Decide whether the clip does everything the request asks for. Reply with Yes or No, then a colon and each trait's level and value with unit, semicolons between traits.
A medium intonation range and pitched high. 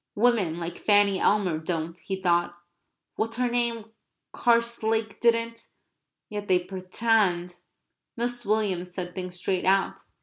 Yes: average, 4.2 semitones; high, 200 Hz